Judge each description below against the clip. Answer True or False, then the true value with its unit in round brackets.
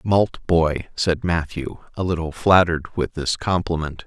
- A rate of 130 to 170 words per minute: True (135 wpm)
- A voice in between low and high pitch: False (85 Hz)